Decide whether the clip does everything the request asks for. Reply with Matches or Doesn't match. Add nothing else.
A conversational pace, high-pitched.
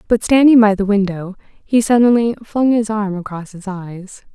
Matches